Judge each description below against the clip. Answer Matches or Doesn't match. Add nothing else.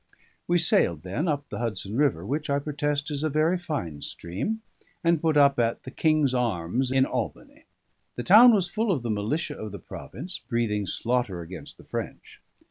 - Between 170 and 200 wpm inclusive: Matches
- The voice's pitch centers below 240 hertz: Matches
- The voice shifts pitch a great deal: Matches